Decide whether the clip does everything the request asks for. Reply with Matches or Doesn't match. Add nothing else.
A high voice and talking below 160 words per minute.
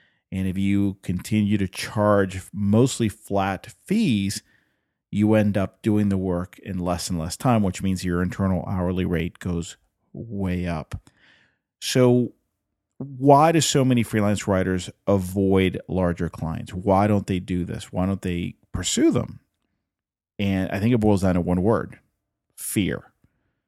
Doesn't match